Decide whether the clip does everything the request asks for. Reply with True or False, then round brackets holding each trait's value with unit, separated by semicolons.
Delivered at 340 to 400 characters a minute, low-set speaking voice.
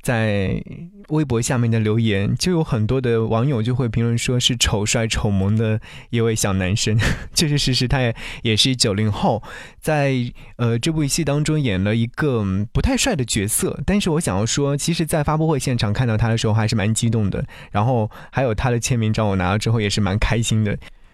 False (300 characters per minute; 115 Hz)